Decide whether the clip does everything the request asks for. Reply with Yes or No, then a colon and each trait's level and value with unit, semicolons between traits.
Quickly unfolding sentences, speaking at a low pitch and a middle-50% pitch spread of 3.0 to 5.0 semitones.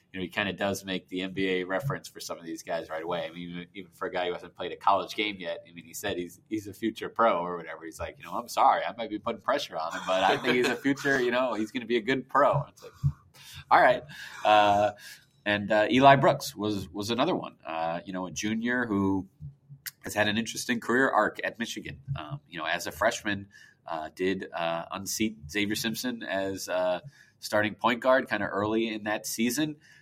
Yes: fast, 235 wpm; low, 105 Hz; average, 3.6 semitones